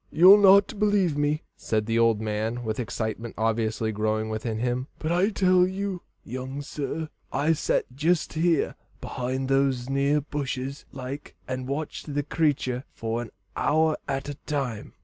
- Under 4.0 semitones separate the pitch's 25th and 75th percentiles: No, average, 5.2 semitones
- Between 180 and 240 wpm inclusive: No, average, 155 wpm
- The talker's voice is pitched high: No, low, 135 Hz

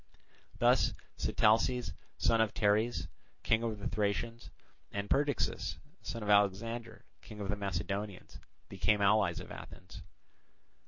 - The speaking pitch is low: Yes, low, 105 Hz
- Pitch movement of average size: No, narrow, 2.2 semitones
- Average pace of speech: No, slow, 120 wpm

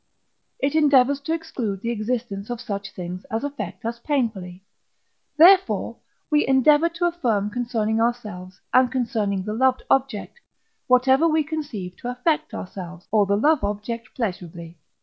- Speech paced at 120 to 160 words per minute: Yes, average, 145 wpm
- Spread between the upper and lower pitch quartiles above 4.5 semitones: Yes, wide, 5.5 semitones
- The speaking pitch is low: No, high, 235 Hz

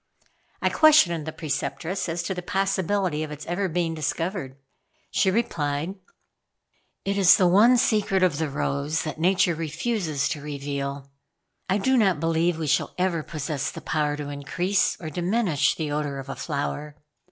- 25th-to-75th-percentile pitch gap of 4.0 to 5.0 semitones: Yes, average, 4.3 semitones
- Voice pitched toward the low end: No, medium, 165 Hz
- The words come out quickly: No, average, 165 wpm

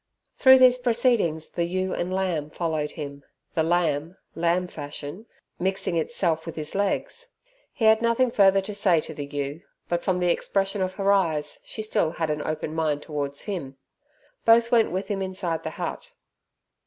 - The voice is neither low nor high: Yes, medium, 175 Hz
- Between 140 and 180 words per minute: Yes, average, 175 wpm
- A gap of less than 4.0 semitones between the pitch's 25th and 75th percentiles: No, average, 4.3 semitones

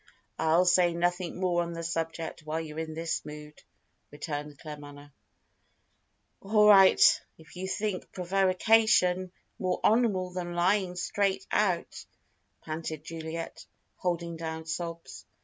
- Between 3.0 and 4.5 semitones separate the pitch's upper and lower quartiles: No, narrow, 2.4 semitones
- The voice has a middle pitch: Yes, medium, 170 Hz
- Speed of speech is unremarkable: No, slow, 120 wpm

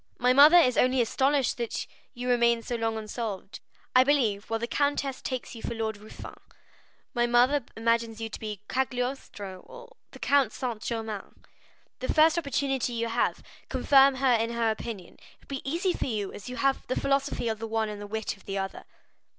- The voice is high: Yes, high, 240 Hz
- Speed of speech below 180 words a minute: No, average, 200 wpm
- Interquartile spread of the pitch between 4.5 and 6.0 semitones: No, average, 3.4 semitones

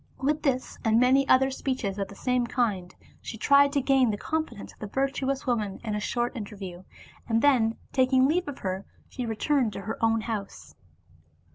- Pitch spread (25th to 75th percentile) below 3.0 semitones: No, average, 4.2 semitones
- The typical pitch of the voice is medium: No, high, 240 Hz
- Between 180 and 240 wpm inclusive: Yes, average, 185 wpm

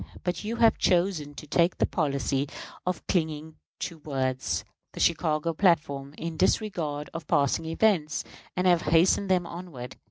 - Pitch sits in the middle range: Yes, medium, 165 Hz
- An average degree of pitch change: Yes, average, 3.5 semitones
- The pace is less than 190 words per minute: Yes, average, 150 wpm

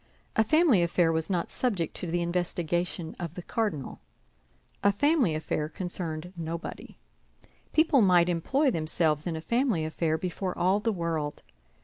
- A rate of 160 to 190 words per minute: No, average, 145 wpm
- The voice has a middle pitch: Yes, medium, 175 Hz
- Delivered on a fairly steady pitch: No, average, 3.9 semitones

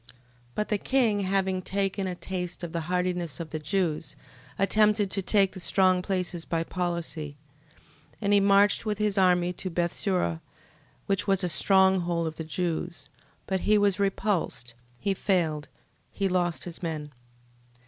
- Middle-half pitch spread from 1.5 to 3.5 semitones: Yes, average, 2.8 semitones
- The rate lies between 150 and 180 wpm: Yes, average, 165 wpm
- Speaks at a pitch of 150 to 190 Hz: Yes, medium, 185 Hz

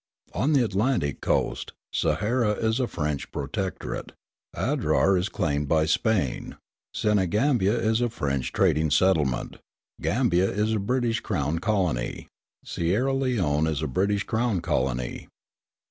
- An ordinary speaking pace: No, slow, 125 wpm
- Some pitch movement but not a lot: No, wide, 6.4 semitones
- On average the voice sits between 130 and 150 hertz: No, very low, 95 Hz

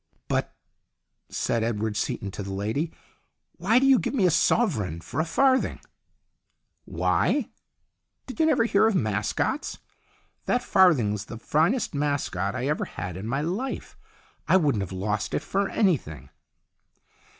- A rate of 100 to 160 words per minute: Yes, average, 150 wpm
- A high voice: No, medium, 140 Hz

